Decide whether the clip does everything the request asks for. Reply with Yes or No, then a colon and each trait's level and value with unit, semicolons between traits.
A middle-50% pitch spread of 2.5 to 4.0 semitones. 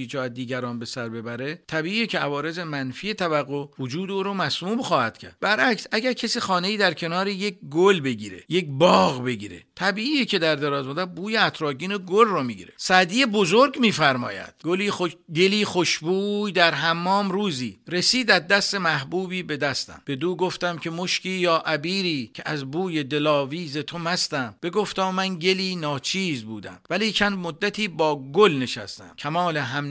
No: average, 5.2 semitones